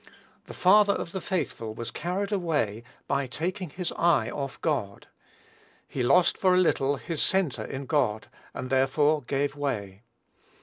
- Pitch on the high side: No, medium, 145 Hz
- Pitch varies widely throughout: Yes, wide, 6.2 semitones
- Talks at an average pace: Yes, average, 150 wpm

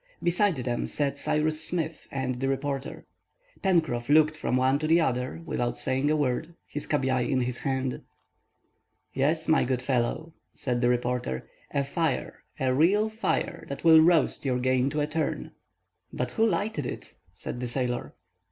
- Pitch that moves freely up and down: No, average, 3.9 semitones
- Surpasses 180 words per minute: No, average, 165 wpm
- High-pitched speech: No, medium, 140 Hz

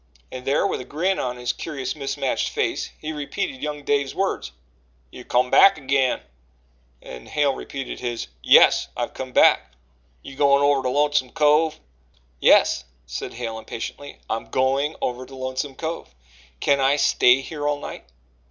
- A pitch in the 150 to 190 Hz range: No, low, 135 Hz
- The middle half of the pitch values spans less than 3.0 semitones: Yes, narrow, 2.6 semitones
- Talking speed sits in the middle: Yes, average, 160 wpm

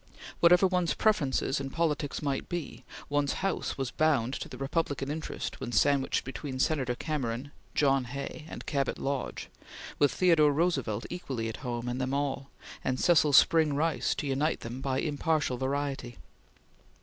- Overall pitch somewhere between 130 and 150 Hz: Yes, medium, 140 Hz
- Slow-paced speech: No, average, 155 wpm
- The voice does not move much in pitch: No, average, 3.0 semitones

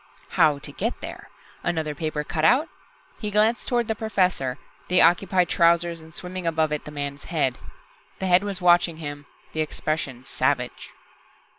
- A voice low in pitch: No, medium, 165 Hz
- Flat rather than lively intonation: No, average, 3.7 semitones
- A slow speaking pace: No, average, 155 wpm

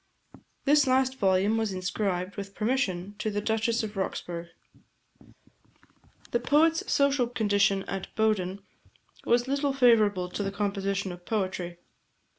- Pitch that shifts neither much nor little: Yes, average, 3.9 semitones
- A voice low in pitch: No, high, 205 Hz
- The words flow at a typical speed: No, slow, 125 wpm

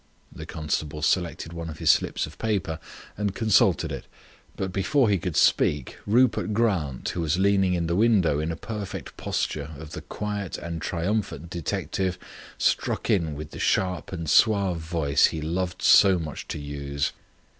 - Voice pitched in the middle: No, very low, 85 Hz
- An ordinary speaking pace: Yes, average, 165 wpm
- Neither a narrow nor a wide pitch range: Yes, average, 4.1 semitones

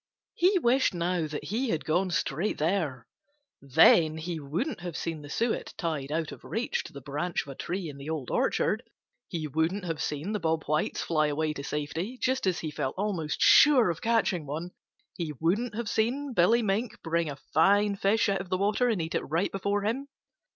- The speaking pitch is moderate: Yes, medium, 175 Hz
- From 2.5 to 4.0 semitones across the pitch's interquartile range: No, average, 5.1 semitones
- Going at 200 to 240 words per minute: Yes, fast, 205 wpm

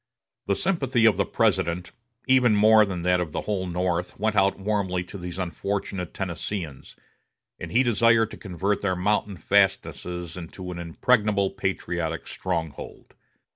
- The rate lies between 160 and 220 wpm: No, average, 145 wpm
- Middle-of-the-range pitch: No, very low, 95 Hz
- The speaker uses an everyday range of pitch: Yes, average, 3.0 semitones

